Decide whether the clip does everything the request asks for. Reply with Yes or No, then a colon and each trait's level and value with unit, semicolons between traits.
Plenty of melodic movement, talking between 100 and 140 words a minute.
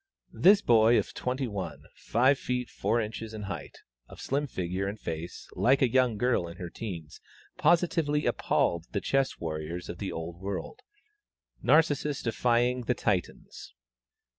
No: wide, 6.3 semitones; average, 150 wpm